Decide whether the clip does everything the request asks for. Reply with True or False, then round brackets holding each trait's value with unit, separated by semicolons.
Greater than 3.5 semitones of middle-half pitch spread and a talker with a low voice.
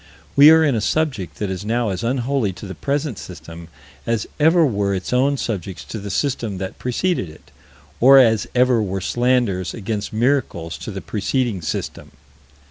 True (5.5 semitones; 115 Hz)